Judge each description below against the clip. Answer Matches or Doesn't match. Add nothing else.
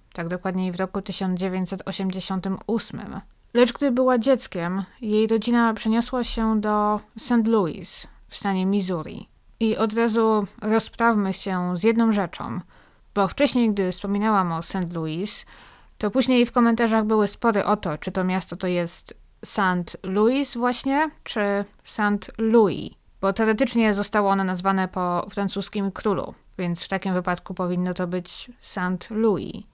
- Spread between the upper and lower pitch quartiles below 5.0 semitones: Matches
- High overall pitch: Matches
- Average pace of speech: Matches